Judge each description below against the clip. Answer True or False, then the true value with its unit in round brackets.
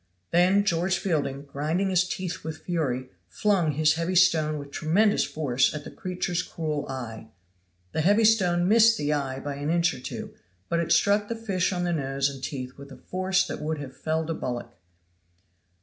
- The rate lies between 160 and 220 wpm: True (190 wpm)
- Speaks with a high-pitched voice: False (160 Hz)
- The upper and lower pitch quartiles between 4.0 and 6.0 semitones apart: True (4.6 semitones)